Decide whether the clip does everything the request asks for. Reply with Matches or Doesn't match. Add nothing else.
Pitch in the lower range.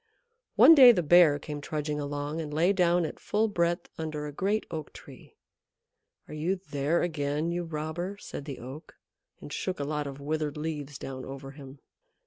Doesn't match